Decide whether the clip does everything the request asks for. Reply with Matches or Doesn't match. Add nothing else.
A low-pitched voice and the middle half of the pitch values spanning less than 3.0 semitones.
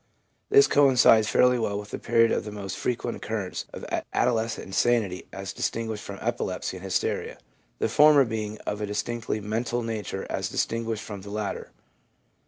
Matches